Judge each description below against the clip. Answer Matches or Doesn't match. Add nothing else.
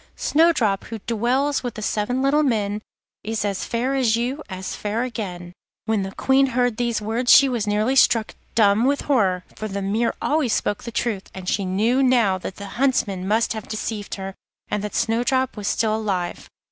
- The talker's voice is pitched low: Doesn't match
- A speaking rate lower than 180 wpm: Doesn't match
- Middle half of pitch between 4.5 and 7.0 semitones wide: Doesn't match